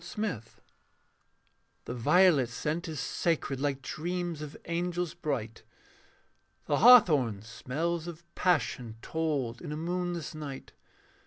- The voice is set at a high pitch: No, medium, 155 Hz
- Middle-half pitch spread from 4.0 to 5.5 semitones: Yes, average, 4.8 semitones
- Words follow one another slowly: Yes, slow, 115 wpm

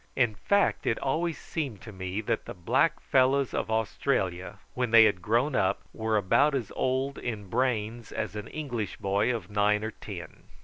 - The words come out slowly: No, average, 180 wpm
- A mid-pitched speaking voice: No, low, 110 Hz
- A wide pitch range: No, average, 4.1 semitones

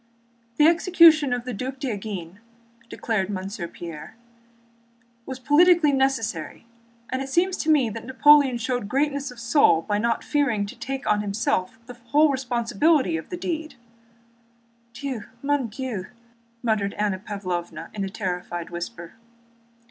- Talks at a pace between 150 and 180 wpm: No, average, 140 wpm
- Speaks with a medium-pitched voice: No, high, 240 Hz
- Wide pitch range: Yes, wide, 5.8 semitones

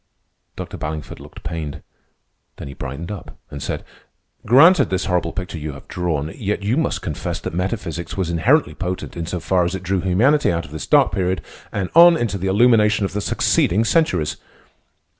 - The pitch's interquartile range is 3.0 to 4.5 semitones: Yes, average, 4.1 semitones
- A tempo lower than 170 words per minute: No, average, 185 wpm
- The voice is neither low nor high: No, very low, 95 Hz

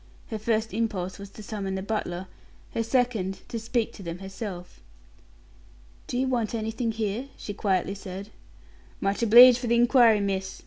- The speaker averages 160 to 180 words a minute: Yes, average, 165 wpm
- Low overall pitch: No, high, 215 Hz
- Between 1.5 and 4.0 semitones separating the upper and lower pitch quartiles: Yes, average, 3.2 semitones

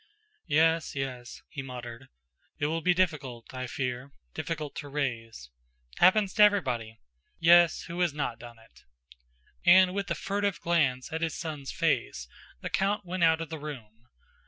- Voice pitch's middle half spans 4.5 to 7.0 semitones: Yes, wide, 5.5 semitones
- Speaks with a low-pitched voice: No, medium, 150 Hz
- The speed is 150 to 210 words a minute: Yes, average, 160 wpm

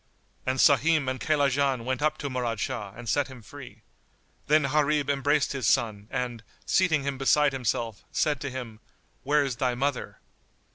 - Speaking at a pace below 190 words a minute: Yes, average, 170 wpm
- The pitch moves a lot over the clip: No, average, 3.0 semitones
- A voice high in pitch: No, low, 135 Hz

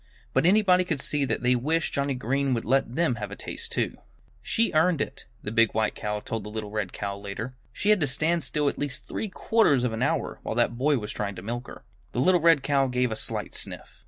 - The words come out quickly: Yes, fast, 245 wpm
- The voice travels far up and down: Yes, wide, 5.8 semitones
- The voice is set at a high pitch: No, low, 130 Hz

